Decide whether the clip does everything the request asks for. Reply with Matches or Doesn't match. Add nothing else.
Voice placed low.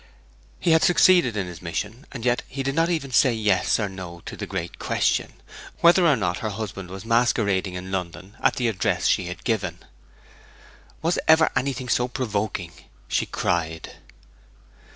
Matches